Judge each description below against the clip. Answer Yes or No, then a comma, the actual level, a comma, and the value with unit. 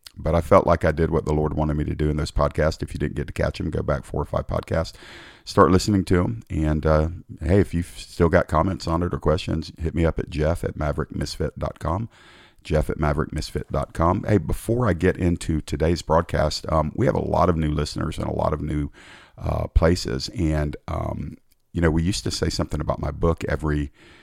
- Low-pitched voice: Yes, very low, 80 Hz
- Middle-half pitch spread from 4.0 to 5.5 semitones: No, average, 2.8 semitones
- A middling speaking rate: No, fast, 225 wpm